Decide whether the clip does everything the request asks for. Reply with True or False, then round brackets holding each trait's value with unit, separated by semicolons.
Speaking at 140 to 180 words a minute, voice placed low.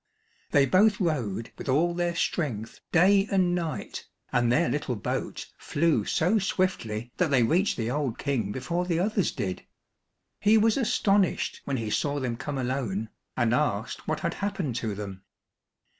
False (160 wpm; 145 Hz)